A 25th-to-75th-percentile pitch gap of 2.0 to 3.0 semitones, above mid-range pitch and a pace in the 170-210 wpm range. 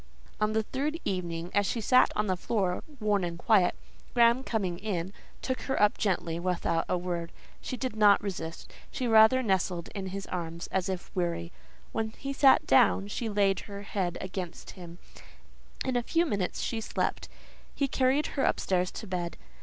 No: average, 4.2 semitones; high, 200 Hz; average, 175 wpm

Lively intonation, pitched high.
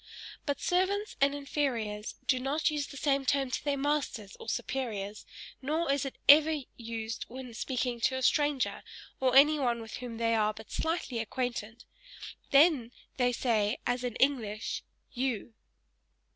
No: average, 3.8 semitones; very high, 260 Hz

